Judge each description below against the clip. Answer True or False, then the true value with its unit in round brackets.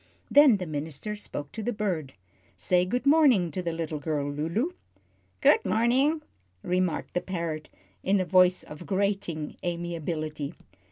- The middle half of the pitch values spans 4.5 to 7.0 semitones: True (5.0 semitones)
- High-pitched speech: False (180 Hz)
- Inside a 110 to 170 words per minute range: True (145 wpm)